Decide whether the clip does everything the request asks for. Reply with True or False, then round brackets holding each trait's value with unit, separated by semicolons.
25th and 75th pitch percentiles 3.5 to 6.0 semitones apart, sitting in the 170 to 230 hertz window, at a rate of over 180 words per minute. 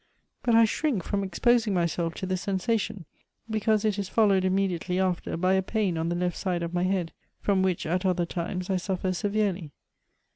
False (2.5 semitones; 190 Hz; 190 wpm)